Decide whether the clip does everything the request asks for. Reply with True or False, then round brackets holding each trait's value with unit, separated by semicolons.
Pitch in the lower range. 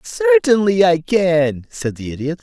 False (185 Hz)